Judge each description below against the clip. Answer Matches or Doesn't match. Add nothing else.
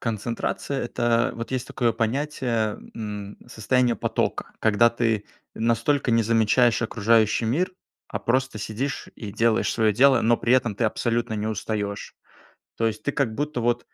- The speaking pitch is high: Doesn't match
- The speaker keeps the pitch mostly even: Matches